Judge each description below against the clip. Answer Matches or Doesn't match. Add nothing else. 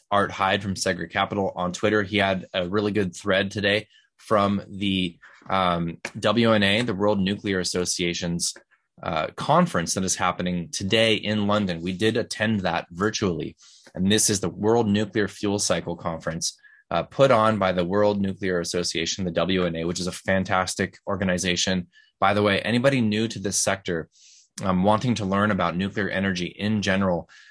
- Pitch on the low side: Matches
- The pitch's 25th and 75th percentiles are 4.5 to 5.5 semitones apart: Doesn't match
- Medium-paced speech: Matches